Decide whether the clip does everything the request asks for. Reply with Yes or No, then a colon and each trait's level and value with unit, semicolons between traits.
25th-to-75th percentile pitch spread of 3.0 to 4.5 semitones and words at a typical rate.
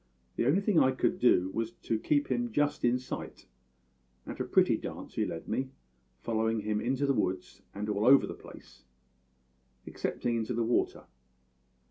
Yes: average, 3.5 semitones; average, 170 wpm